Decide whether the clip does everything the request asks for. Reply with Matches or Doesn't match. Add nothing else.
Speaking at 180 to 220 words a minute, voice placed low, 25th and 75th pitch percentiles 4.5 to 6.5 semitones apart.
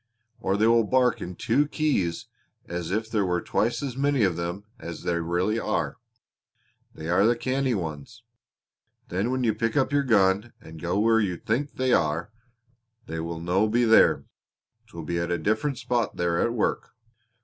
Matches